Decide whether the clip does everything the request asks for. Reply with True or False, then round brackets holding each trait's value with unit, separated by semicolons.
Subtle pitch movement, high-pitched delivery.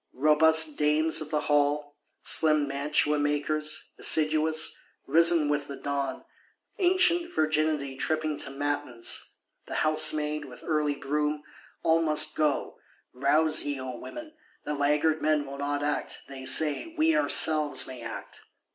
False (1.5 semitones; 150 Hz)